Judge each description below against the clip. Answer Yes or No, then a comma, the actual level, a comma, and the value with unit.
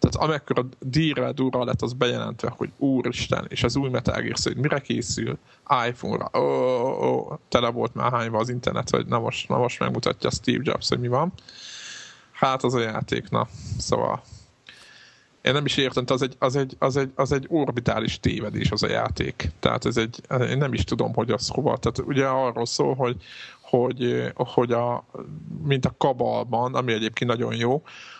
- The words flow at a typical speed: No, fast, 185 wpm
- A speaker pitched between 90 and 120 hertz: No, low, 130 Hz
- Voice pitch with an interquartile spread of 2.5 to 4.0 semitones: Yes, average, 2.9 semitones